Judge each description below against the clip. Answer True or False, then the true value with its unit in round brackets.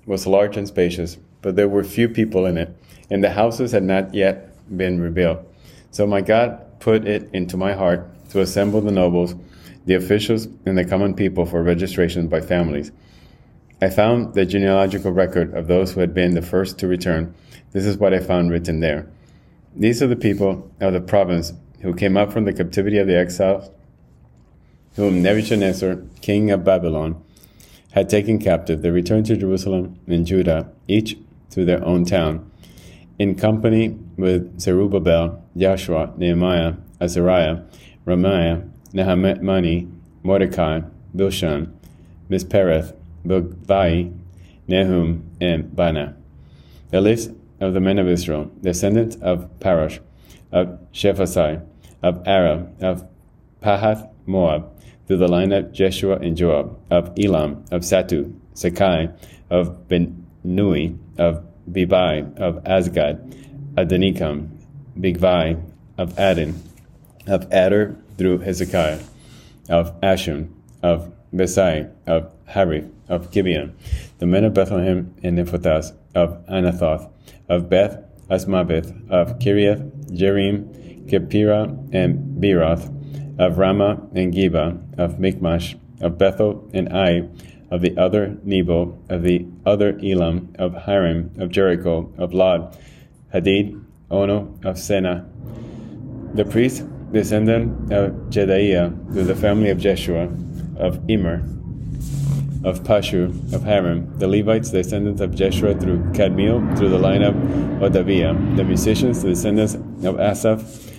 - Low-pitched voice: True (95 Hz)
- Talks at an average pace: False (130 wpm)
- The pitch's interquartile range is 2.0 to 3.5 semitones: True (2.7 semitones)